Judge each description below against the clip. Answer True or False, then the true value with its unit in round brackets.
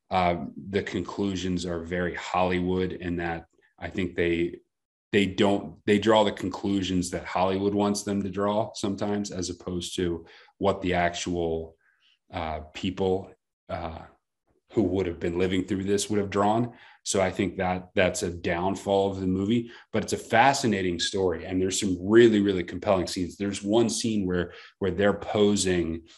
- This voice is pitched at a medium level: False (95 Hz)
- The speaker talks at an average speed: True (165 wpm)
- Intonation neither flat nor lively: False (2.2 semitones)